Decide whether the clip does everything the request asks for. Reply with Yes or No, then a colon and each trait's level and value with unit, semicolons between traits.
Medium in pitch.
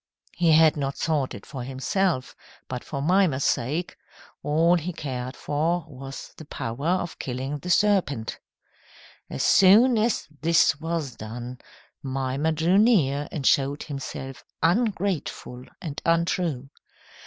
Yes: medium, 150 Hz